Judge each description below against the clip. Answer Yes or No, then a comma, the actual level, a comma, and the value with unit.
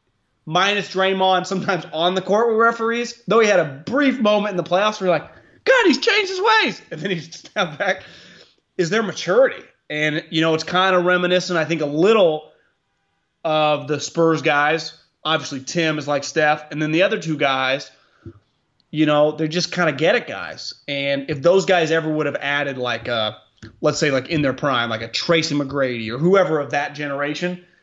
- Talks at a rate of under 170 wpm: No, average, 200 wpm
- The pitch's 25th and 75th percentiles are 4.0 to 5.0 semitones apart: Yes, average, 4.4 semitones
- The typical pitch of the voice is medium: Yes, medium, 160 Hz